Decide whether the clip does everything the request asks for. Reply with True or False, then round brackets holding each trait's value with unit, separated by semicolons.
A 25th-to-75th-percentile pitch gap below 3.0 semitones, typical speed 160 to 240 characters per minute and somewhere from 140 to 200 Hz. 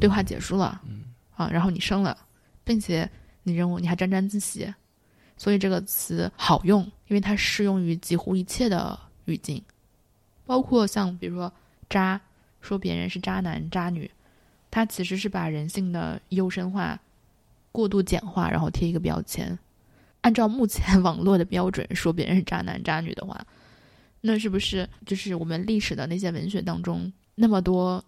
False (2.5 semitones; 250 characters per minute; 185 Hz)